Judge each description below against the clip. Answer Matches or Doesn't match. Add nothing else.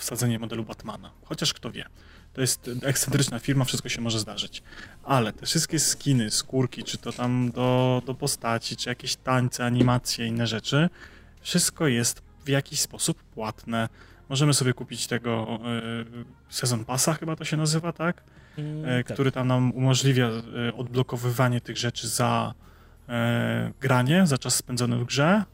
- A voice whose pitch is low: Matches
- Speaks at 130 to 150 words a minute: Matches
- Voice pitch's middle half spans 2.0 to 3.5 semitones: Matches